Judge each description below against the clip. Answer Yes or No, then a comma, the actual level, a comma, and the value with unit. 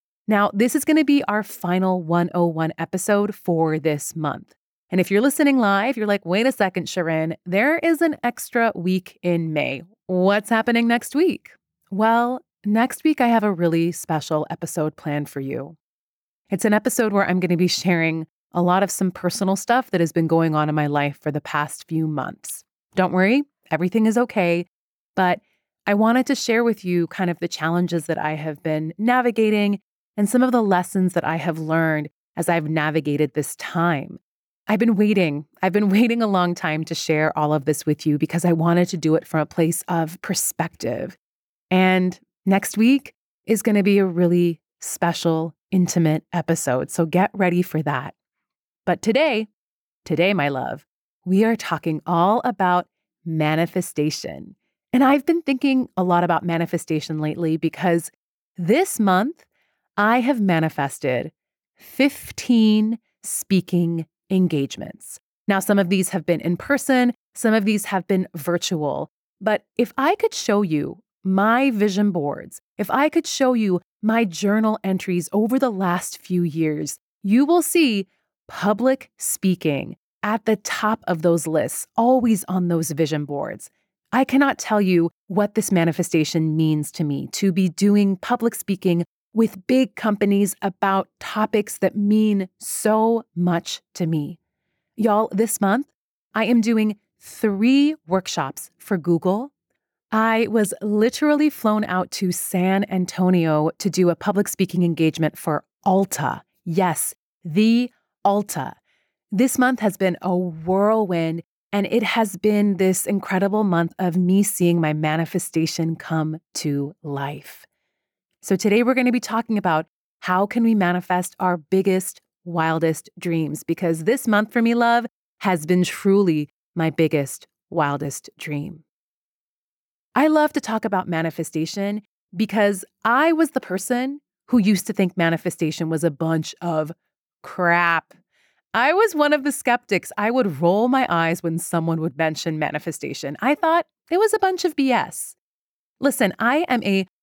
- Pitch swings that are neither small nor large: Yes, average, 4.9 semitones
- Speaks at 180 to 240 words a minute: No, average, 160 wpm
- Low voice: No, medium, 185 Hz